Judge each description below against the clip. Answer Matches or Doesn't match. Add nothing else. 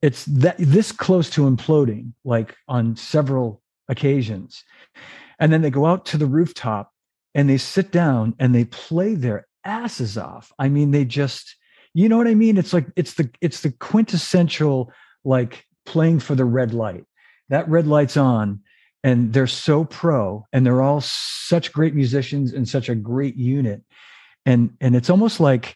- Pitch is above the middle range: Doesn't match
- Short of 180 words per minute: Matches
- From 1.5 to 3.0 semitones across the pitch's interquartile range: Doesn't match